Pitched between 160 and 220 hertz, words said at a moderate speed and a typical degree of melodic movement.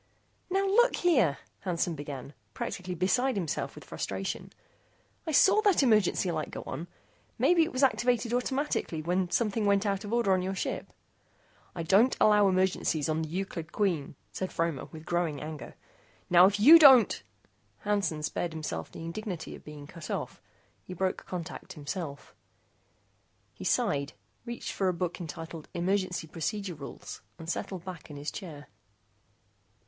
Yes: medium, 185 Hz; average, 155 wpm; average, 4.7 semitones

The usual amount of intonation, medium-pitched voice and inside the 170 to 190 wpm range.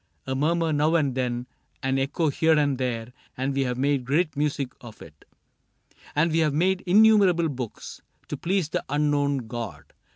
Yes: average, 3.8 semitones; medium, 145 Hz; average, 175 wpm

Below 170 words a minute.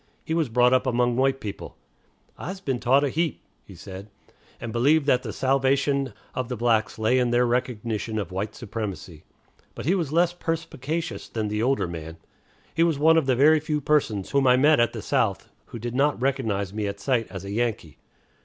No: average, 200 wpm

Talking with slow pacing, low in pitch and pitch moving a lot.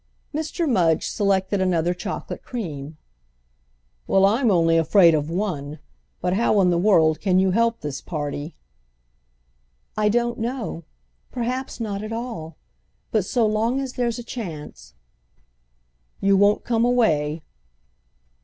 No: slow, 125 wpm; high, 195 Hz; wide, 6.1 semitones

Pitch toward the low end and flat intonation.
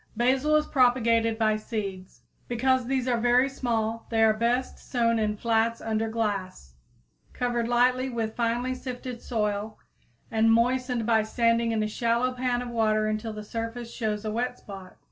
No: high, 230 Hz; narrow, 2.2 semitones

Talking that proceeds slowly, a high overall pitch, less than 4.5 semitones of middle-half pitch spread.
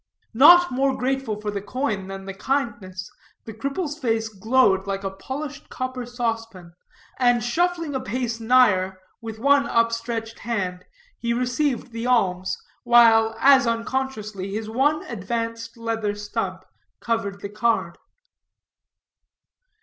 Yes: slow, 125 wpm; high, 230 Hz; average, 3.8 semitones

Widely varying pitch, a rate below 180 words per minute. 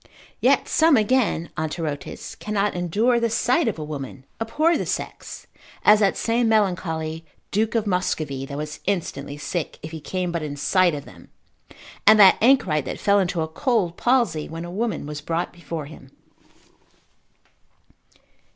Yes: wide, 5.8 semitones; average, 160 wpm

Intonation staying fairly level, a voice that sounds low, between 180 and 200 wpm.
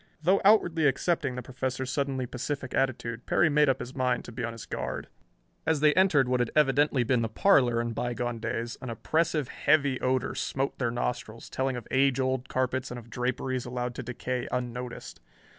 Yes: narrow, 2.1 semitones; low, 130 Hz; average, 190 wpm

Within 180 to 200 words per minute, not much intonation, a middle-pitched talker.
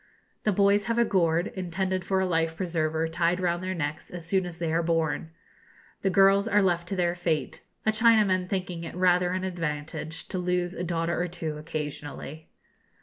Yes: average, 190 wpm; narrow, 2.3 semitones; medium, 175 Hz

